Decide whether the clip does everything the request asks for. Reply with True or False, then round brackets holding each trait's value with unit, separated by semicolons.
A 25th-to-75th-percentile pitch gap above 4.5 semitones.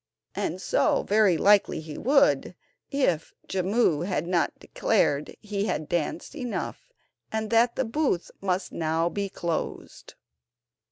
True (5.2 semitones)